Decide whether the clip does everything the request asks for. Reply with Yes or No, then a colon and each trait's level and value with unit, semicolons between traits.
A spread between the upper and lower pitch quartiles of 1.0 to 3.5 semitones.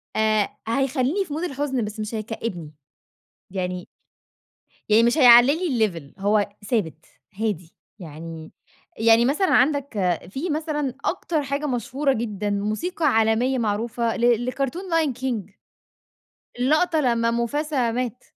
No: average, 4.7 semitones